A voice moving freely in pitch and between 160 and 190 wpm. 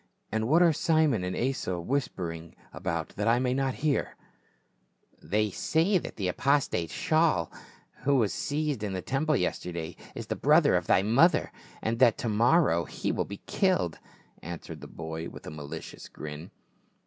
Yes: wide, 8.6 semitones; average, 170 wpm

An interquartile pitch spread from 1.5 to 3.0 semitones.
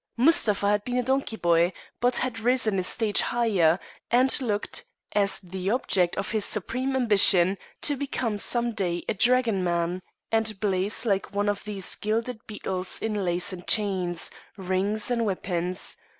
No: average, 4.0 semitones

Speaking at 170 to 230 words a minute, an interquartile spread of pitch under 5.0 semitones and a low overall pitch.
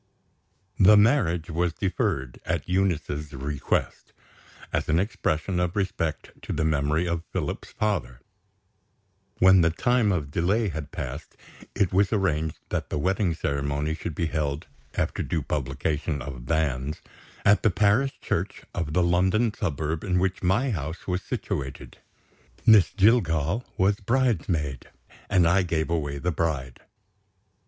No: average, 140 wpm; average, 4.4 semitones; very low, 85 Hz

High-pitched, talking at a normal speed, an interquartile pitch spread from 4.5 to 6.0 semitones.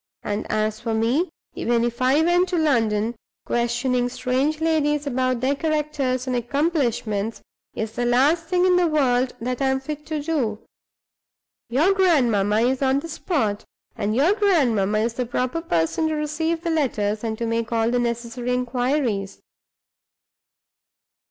Yes: very high, 255 Hz; average, 155 wpm; average, 4.9 semitones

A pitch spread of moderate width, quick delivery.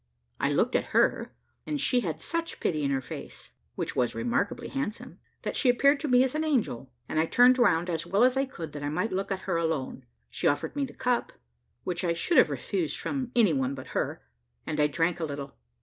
No: wide, 8.8 semitones; fast, 230 wpm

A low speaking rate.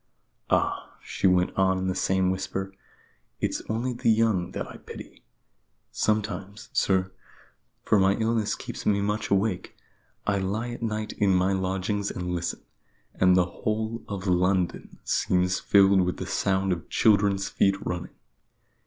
No: average, 150 wpm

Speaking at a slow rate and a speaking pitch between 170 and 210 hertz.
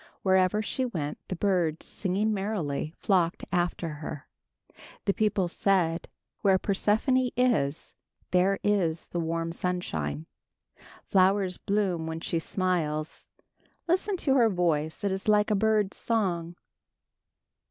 Yes: slow, 120 wpm; medium, 185 Hz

